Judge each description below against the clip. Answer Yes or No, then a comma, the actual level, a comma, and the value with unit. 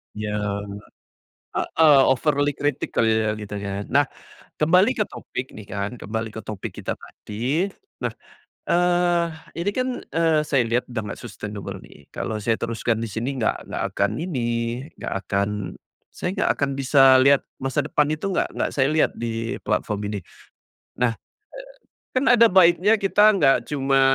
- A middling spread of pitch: No, wide, 6.7 semitones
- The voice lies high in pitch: No, low, 135 Hz